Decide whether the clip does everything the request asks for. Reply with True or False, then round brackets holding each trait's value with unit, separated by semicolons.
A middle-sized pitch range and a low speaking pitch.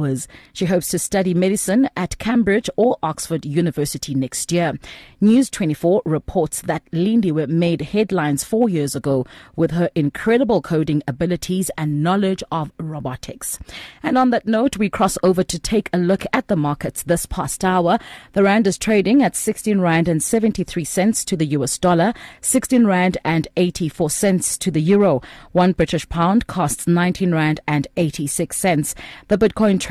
False (4.3 semitones; 180 Hz)